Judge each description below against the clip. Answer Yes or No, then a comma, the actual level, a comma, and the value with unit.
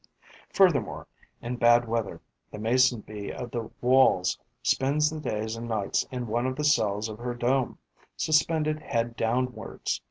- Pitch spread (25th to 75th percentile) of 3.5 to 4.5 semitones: No, average, 3.0 semitones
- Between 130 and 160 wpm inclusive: Yes, average, 155 wpm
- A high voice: No, low, 120 Hz